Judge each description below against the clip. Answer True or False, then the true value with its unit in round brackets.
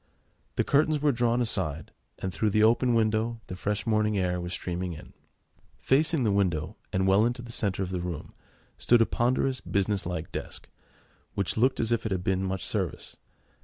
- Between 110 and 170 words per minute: False (190 wpm)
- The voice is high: False (105 Hz)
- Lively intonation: False (4.3 semitones)